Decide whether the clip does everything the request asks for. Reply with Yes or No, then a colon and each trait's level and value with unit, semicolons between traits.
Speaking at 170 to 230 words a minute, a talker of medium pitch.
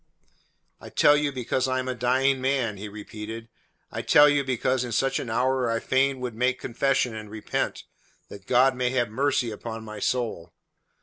No: average, 190 wpm; low, 125 Hz